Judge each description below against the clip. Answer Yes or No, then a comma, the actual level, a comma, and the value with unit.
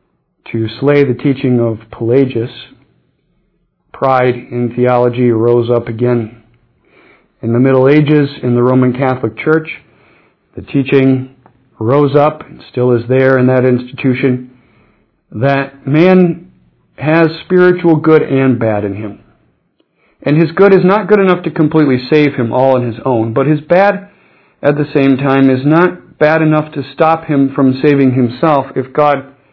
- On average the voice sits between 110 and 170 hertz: Yes, low, 135 Hz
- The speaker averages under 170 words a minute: Yes, average, 150 wpm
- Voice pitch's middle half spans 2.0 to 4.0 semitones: Yes, average, 3.7 semitones